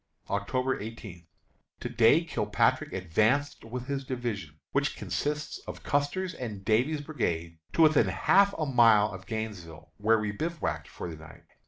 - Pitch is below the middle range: Yes, low, 115 Hz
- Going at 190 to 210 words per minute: No, average, 150 wpm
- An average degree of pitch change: No, wide, 6.2 semitones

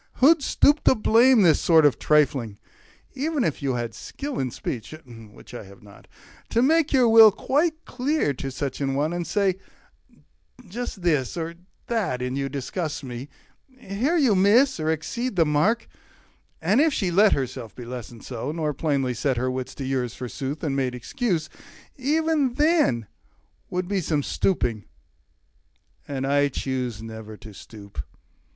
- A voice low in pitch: No, medium, 155 Hz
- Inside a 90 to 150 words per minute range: No, average, 165 wpm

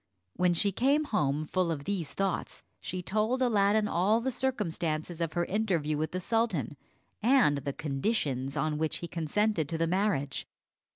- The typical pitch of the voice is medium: Yes, medium, 175 Hz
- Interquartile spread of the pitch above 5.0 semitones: Yes, wide, 5.6 semitones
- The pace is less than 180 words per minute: Yes, average, 165 wpm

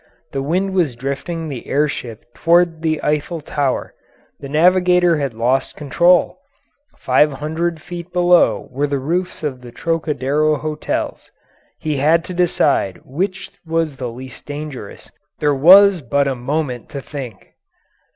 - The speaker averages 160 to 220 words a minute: No, average, 140 wpm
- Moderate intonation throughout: Yes, average, 4.0 semitones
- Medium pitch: Yes, medium, 150 Hz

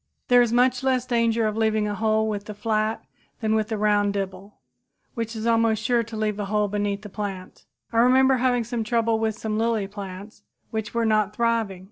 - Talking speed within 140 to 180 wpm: No, average, 200 wpm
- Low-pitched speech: No, high, 220 Hz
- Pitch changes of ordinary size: No, narrow, 1.9 semitones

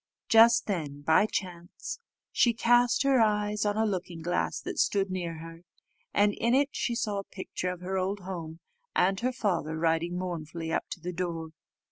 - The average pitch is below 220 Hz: Yes, medium, 185 Hz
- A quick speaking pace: No, average, 180 wpm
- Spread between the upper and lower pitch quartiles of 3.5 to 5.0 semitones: Yes, average, 3.9 semitones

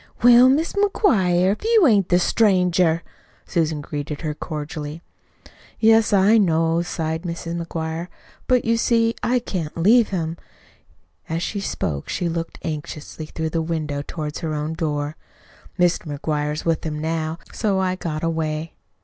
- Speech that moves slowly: No, average, 150 wpm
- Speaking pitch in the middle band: Yes, medium, 165 Hz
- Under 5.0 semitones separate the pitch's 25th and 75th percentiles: Yes, average, 3.9 semitones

